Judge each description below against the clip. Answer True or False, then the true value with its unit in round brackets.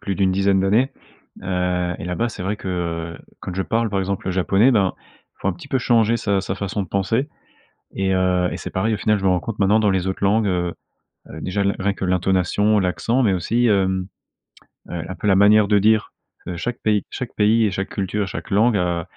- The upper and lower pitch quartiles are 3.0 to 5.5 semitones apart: False (2.6 semitones)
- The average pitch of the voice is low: True (95 Hz)